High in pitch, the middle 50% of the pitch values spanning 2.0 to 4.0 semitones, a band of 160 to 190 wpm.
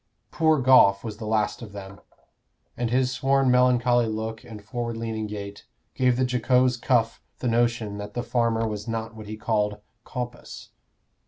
No: low, 115 Hz; narrow, 2.5 semitones; average, 165 wpm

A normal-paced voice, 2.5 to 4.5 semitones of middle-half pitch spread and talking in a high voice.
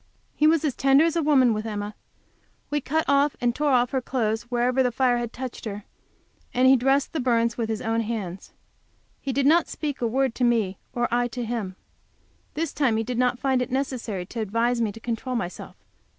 No: fast, 215 wpm; average, 3.0 semitones; high, 245 Hz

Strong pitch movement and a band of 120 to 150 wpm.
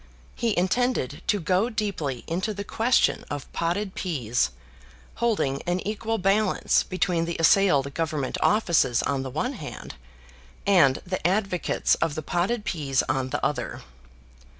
Yes: wide, 6.3 semitones; average, 140 wpm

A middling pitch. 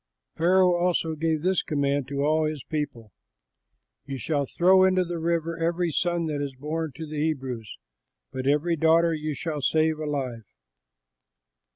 Yes: medium, 155 Hz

